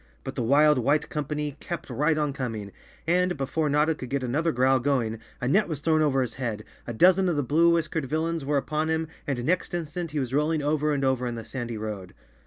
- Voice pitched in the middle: Yes, medium, 145 Hz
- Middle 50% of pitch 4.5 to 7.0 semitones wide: No, average, 3.8 semitones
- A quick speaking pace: Yes, fast, 230 wpm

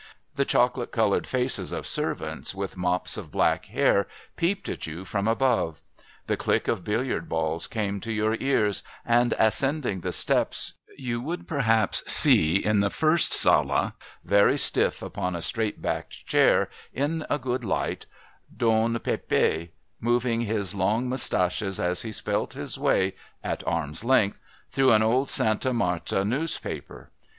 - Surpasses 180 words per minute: No, average, 150 wpm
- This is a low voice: Yes, low, 110 Hz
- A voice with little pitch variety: No, average, 4.4 semitones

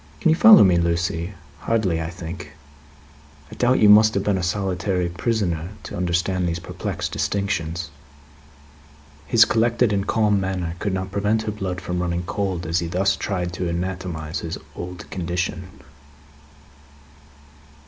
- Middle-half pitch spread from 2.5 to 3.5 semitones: Yes, average, 2.8 semitones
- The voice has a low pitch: Yes, very low, 90 Hz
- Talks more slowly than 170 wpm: Yes, average, 150 wpm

